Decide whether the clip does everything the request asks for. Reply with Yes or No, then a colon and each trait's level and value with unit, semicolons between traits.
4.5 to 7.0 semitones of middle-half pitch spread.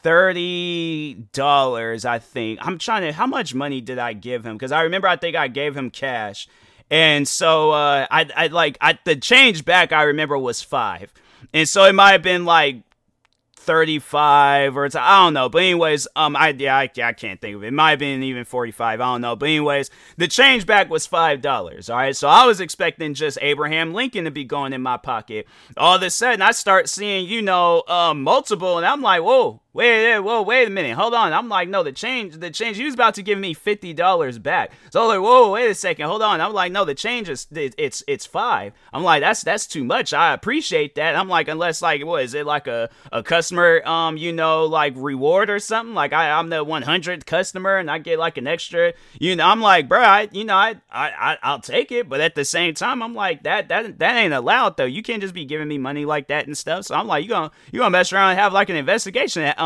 Yes: wide, 5.4 semitones